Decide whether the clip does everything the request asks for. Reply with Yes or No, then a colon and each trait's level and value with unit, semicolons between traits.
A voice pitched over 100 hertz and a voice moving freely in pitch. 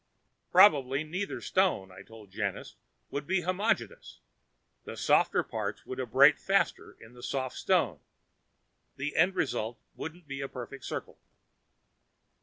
Yes: medium, 140 Hz; wide, 6.7 semitones